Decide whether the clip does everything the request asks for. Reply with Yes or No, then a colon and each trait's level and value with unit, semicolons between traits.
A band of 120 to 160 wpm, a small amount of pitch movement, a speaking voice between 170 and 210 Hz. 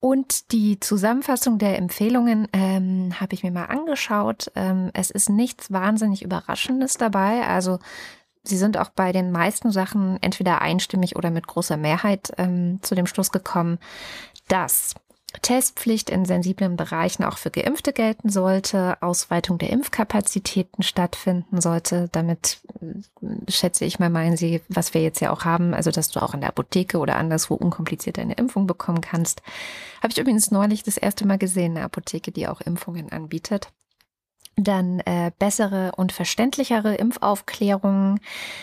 No: average, 150 wpm; average, 3.1 semitones; high, 190 Hz